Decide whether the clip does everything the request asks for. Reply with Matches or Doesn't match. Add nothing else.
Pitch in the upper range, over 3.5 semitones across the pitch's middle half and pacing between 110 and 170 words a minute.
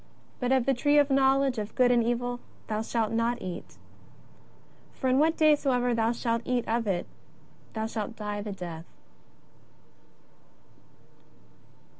Doesn't match